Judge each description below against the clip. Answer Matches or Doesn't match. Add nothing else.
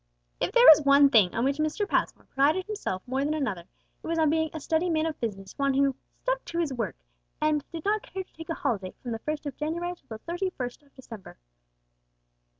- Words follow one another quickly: Matches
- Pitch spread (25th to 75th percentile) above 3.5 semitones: Matches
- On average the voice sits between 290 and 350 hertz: Matches